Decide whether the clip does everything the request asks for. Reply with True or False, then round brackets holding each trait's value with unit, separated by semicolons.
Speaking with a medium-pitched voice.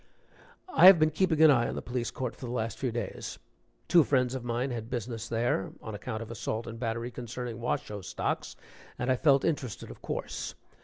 False (120 Hz)